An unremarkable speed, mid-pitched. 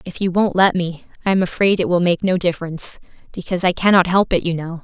No: fast, 250 wpm; medium, 180 Hz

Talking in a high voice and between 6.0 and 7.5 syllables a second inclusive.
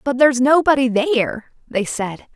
Yes: very high, 255 Hz; 6.3 syllables/s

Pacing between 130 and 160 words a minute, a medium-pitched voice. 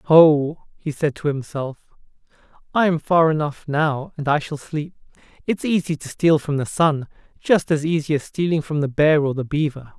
No: average, 185 wpm; medium, 150 Hz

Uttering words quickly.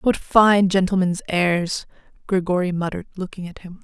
No: average, 140 wpm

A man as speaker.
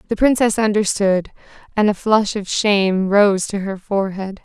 No: female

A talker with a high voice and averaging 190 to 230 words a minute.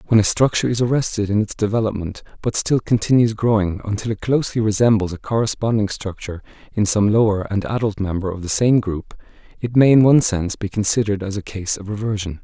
No: low, 105 Hz; average, 200 wpm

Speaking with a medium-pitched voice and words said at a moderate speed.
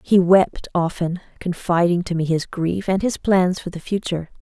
Yes: medium, 175 Hz; average, 190 wpm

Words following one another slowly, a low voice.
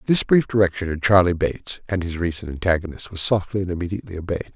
No: average, 200 wpm; very low, 90 Hz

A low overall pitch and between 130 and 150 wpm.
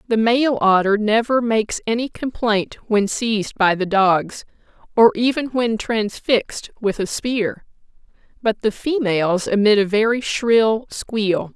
No: high, 220 Hz; average, 140 wpm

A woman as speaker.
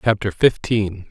No: male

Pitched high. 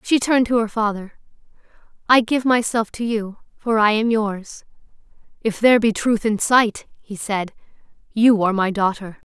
Yes: high, 220 Hz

